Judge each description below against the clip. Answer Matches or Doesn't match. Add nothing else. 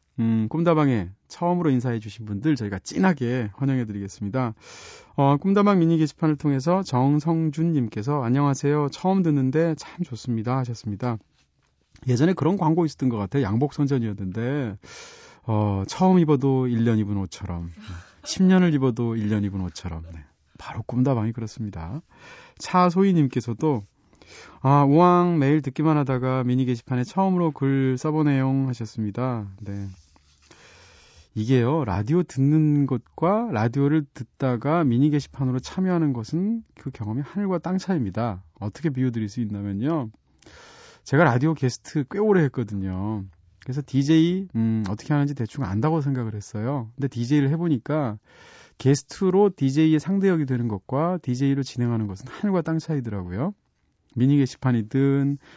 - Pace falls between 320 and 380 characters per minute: Matches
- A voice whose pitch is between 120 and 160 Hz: Matches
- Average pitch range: Doesn't match